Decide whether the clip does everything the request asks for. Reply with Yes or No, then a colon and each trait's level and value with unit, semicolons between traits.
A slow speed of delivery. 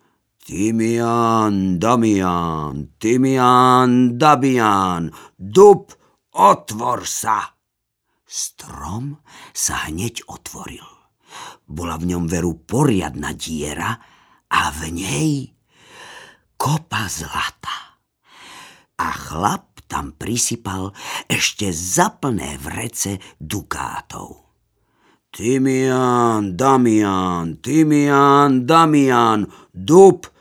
Yes: slow, 70 wpm